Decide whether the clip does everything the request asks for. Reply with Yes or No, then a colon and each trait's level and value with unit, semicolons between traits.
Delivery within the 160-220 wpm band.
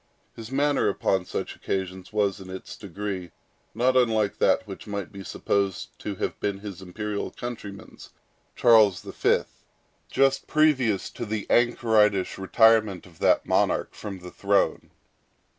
No: average, 140 wpm